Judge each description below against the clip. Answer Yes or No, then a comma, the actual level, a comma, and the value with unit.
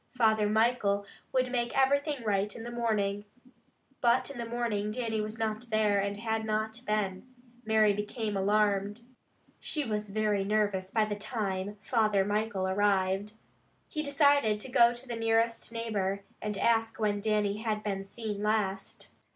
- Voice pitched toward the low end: No, high, 215 Hz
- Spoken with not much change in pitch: Yes, narrow, 2.1 semitones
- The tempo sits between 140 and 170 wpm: Yes, average, 155 wpm